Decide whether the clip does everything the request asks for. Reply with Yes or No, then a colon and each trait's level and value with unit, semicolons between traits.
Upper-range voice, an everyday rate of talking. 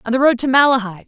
No: high, 245 Hz; fast, 280 wpm